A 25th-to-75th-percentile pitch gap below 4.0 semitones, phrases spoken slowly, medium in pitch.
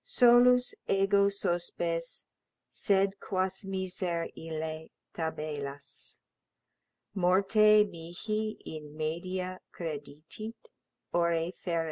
Yes: average, 3.5 semitones; slow, 75 wpm; medium, 180 Hz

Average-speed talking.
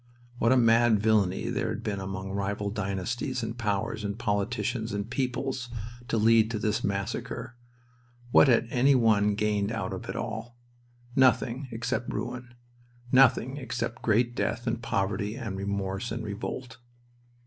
Yes: average, 150 wpm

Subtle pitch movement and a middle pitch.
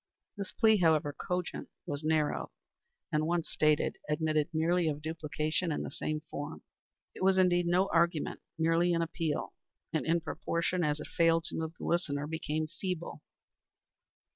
Yes: narrow, 2.2 semitones; medium, 165 Hz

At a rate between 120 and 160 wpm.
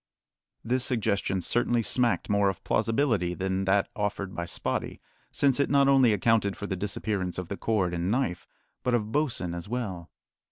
No: average, 170 wpm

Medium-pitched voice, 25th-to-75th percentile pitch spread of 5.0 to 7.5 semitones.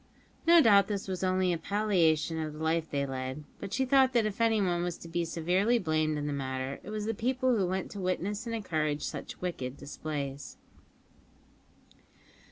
Yes: medium, 180 Hz; wide, 5.5 semitones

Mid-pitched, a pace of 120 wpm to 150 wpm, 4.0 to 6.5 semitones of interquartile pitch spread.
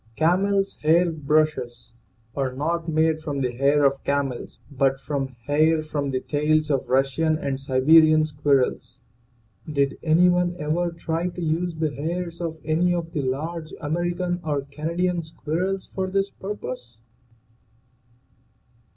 No: medium, 155 Hz; average, 140 wpm; average, 3.4 semitones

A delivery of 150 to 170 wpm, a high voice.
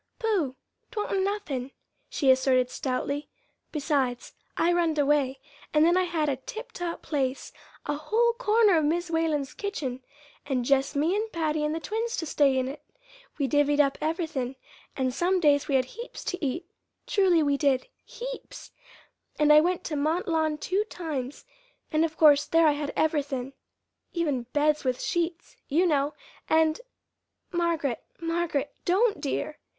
Yes: average, 160 wpm; very high, 305 Hz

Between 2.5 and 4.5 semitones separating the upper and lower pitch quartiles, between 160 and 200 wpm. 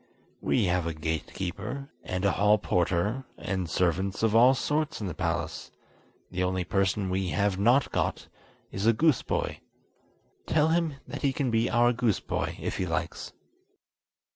No: average, 5.3 semitones; average, 165 wpm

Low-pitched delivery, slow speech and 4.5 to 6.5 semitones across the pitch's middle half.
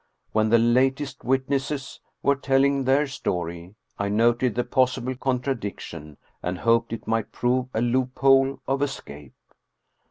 No: low, 125 Hz; slow, 130 wpm; average, 3.2 semitones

